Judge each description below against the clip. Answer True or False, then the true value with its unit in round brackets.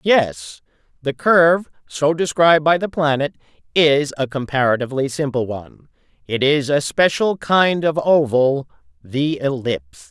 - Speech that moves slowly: True (125 wpm)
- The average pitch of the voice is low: False (145 Hz)